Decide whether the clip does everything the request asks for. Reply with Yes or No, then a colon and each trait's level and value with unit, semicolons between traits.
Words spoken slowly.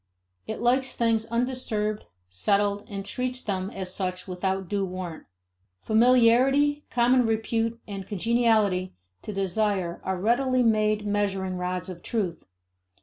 Yes: slow, 125 wpm